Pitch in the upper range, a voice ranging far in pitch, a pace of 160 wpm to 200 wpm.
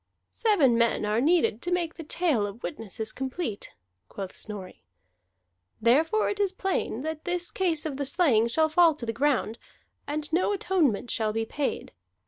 Yes: very high, 295 Hz; wide, 7.4 semitones; average, 170 wpm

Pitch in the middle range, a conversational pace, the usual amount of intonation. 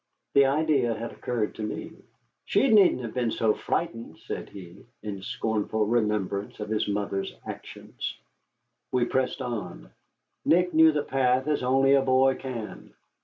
No: low, 120 Hz; average, 150 wpm; average, 4.1 semitones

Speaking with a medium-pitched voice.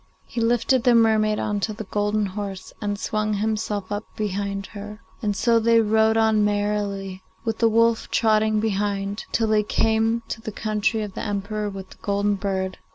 No: high, 210 Hz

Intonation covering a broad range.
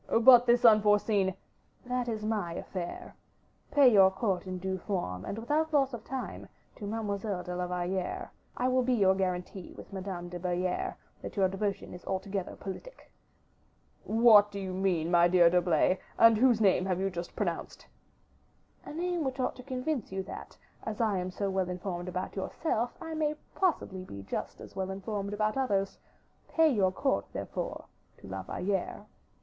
No: average, 4.3 semitones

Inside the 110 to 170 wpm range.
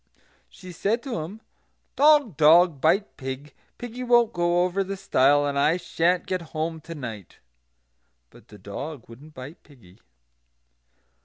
Yes: average, 145 wpm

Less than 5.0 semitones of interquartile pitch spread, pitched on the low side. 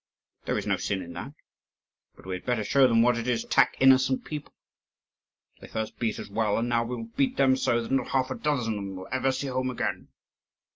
Yes: average, 2.8 semitones; low, 120 Hz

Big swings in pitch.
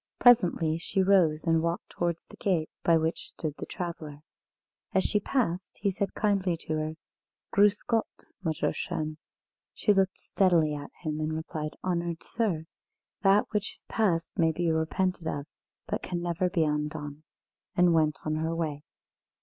No: average, 3.2 semitones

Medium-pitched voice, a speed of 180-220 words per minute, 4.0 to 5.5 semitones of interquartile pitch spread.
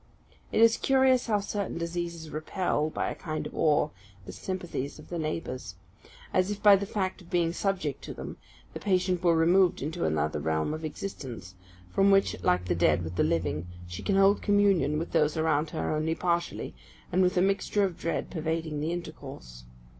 Yes: medium, 165 Hz; average, 190 wpm; average, 4.4 semitones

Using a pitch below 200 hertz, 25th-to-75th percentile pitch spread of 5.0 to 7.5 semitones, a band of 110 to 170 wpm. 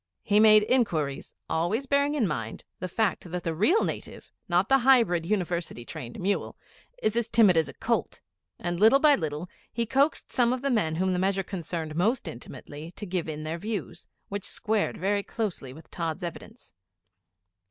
No: high, 190 Hz; wide, 5.4 semitones; average, 180 wpm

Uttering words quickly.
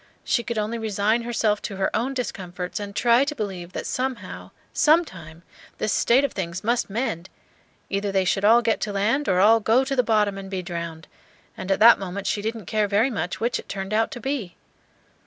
Yes: fast, 210 wpm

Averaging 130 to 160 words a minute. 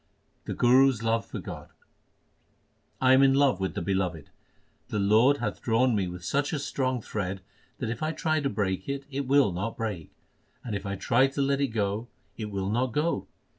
No: fast, 205 wpm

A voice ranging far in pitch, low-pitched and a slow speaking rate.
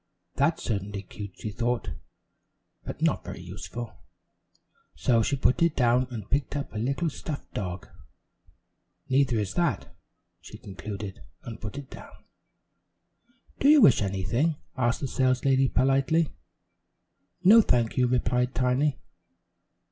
No: average, 4.3 semitones; low, 125 Hz; slow, 130 wpm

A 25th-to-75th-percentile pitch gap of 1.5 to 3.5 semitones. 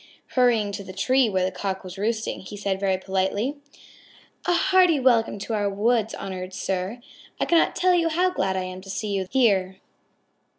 No: average, 4.8 semitones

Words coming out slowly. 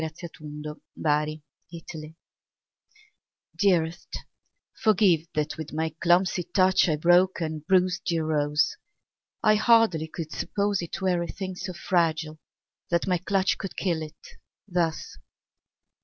Yes: slow, 115 wpm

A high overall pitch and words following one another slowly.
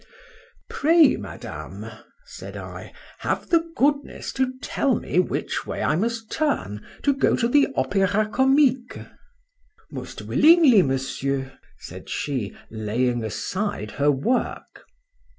Yes: high, 230 Hz; slow, 115 wpm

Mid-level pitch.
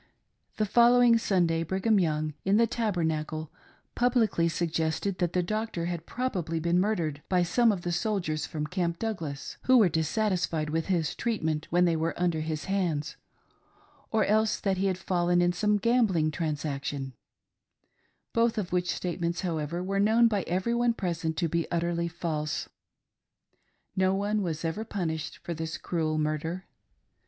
Yes: medium, 175 Hz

